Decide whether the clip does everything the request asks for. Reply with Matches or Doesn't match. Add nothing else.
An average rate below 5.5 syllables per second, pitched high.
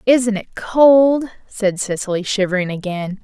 Matches